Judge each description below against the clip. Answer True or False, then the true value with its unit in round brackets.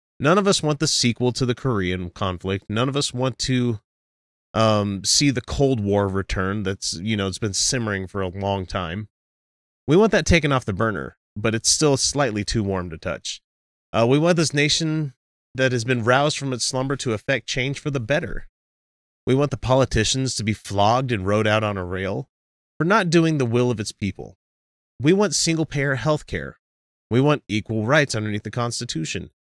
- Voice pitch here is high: False (115 Hz)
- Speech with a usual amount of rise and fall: False (5.9 semitones)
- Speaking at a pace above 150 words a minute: True (200 wpm)